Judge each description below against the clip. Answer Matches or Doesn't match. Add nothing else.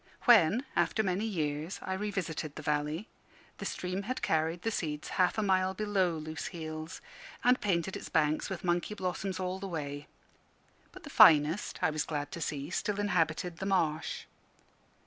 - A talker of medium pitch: Matches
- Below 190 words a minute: Matches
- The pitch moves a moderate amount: Matches